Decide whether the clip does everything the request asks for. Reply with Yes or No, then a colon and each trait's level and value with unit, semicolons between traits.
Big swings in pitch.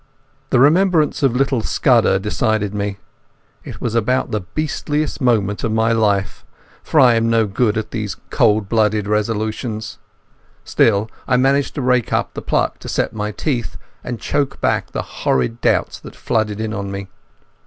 No: average, 3.2 semitones